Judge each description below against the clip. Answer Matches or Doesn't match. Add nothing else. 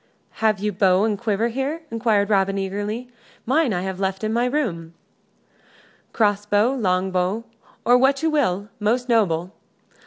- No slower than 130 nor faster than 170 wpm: Matches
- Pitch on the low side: Doesn't match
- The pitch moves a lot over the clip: Doesn't match